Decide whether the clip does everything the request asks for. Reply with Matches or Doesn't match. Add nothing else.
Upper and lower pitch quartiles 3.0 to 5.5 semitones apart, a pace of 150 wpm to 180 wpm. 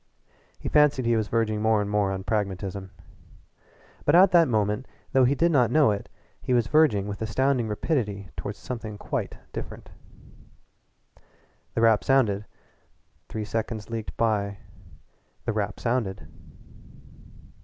Doesn't match